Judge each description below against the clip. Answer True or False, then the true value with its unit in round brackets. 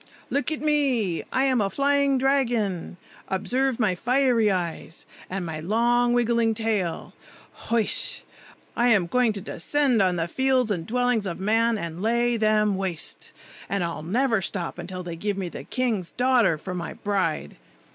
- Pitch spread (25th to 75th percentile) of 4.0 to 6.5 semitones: True (5.1 semitones)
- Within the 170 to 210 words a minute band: False (160 wpm)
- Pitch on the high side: True (220 Hz)